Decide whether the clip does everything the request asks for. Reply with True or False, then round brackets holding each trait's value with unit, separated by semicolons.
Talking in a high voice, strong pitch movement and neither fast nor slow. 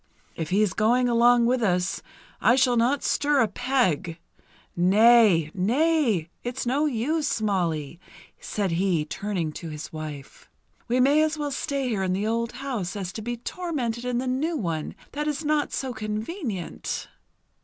True (230 Hz; 6.3 semitones; 160 wpm)